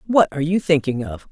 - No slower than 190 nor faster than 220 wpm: No, fast, 230 wpm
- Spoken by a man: No, female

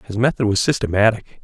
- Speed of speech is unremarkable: Yes, average, 165 wpm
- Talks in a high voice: No, low, 110 Hz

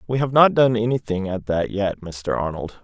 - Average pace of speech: No, fast, 210 wpm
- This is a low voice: Yes, low, 105 Hz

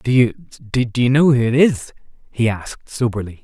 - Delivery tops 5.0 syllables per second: No, 4.8 syllables/s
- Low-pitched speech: Yes, low, 120 Hz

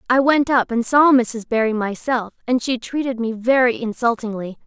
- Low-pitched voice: No, high, 240 Hz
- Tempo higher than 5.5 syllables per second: No, 4.9 syllables/s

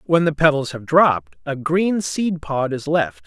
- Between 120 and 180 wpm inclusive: No, average, 200 wpm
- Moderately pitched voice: Yes, medium, 150 Hz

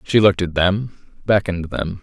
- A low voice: Yes, very low, 95 Hz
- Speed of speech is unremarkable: Yes, average, 175 wpm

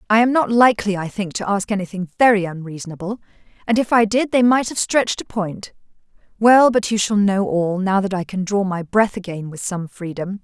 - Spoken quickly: Yes, fast, 220 wpm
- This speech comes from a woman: Yes, female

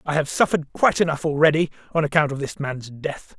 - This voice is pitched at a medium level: Yes, medium, 150 Hz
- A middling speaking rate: No, fast, 215 wpm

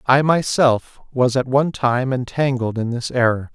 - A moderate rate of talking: Yes, average, 170 wpm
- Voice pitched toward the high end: No, low, 125 Hz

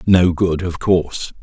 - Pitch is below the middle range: Yes, very low, 85 Hz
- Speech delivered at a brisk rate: No, average, 170 wpm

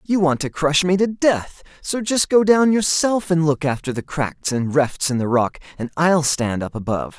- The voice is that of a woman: No, male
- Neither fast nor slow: No, fast, 225 wpm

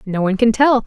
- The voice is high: Yes, high, 225 Hz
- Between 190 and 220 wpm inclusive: No, fast, 275 wpm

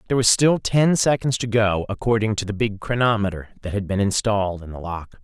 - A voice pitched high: No, low, 110 Hz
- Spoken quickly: Yes, fast, 220 wpm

